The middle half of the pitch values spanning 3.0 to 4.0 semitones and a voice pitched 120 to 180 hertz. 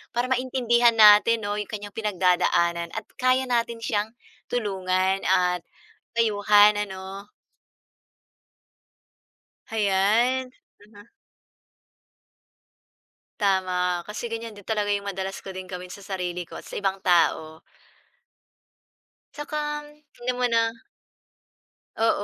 No: average, 3.5 semitones; high, 205 Hz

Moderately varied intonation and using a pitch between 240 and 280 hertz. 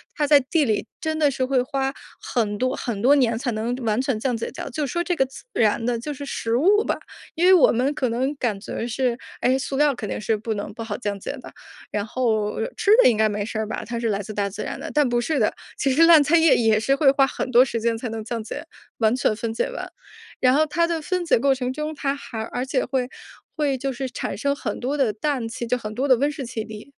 Yes: average, 3.9 semitones; very high, 250 Hz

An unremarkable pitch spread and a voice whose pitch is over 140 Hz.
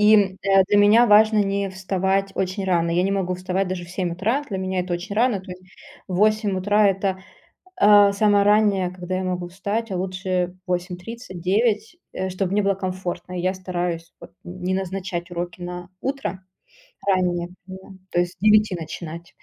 No: narrow, 2.2 semitones; high, 190 Hz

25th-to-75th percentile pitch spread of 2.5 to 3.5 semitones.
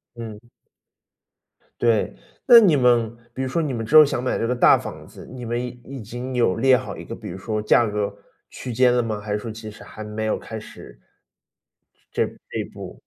Yes: average, 2.9 semitones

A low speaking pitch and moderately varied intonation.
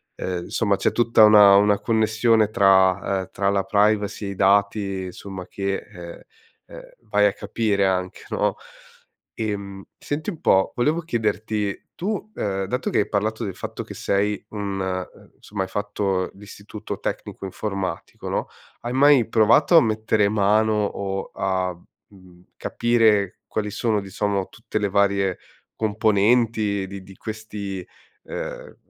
No: low, 100 Hz; narrow, 2.0 semitones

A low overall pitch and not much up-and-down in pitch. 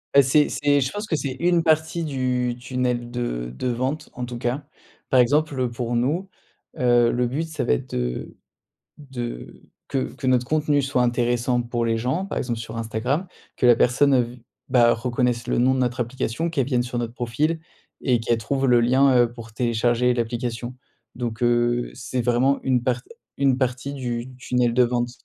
Yes: low, 125 Hz; narrow, 2.1 semitones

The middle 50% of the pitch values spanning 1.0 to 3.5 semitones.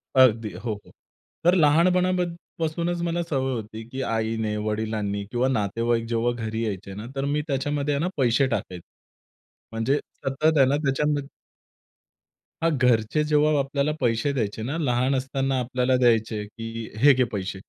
No: average, 4.5 semitones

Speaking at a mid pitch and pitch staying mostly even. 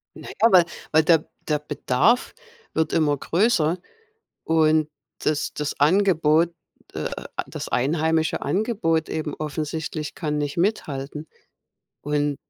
Yes: medium, 155 Hz; narrow, 1.9 semitones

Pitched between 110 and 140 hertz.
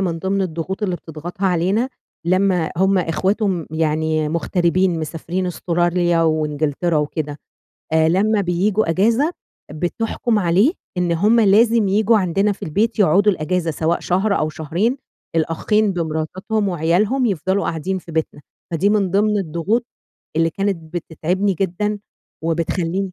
No: medium, 180 Hz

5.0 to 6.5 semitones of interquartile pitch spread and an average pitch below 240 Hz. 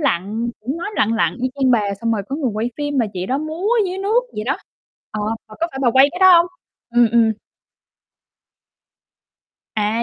No: wide, 5.4 semitones; very high, 250 Hz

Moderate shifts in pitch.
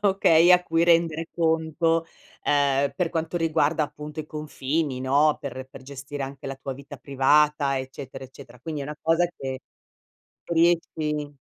Yes: average, 3.1 semitones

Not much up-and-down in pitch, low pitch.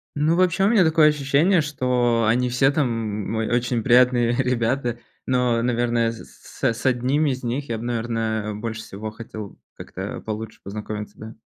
No: average, 3.1 semitones; low, 120 Hz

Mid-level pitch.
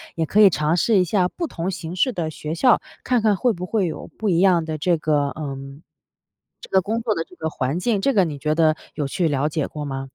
Yes: medium, 170 Hz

